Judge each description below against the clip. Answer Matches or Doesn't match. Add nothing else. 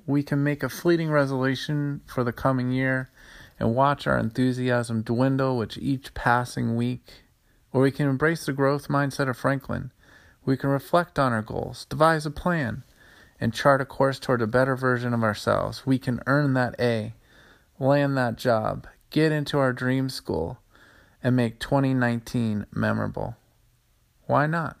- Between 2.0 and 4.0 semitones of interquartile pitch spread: Matches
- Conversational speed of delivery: Matches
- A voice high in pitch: Doesn't match